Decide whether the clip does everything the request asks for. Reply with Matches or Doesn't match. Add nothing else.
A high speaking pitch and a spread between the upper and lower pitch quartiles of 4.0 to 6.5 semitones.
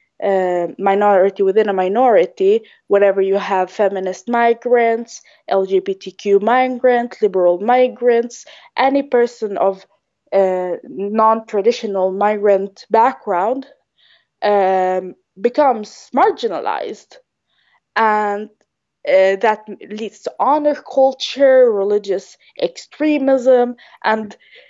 Matches